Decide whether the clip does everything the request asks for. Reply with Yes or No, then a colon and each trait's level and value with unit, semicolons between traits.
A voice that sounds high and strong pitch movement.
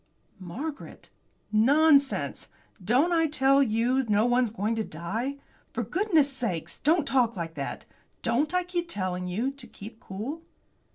Yes: very high, 250 Hz; wide, 5.7 semitones